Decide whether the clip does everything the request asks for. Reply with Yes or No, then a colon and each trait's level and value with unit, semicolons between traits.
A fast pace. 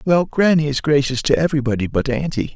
No: average, 190 wpm